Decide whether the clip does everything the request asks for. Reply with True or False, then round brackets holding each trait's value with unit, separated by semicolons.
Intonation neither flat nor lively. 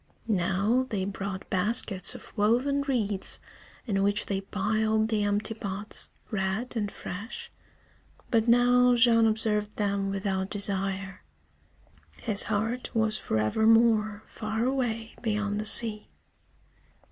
False (2.3 semitones)